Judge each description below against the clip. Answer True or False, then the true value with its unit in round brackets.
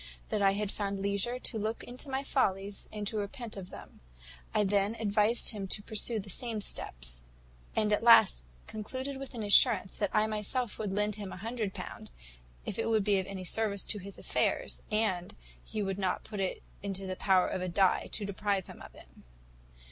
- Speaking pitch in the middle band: False (205 Hz)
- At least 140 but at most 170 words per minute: False (200 wpm)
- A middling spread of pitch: False (2.2 semitones)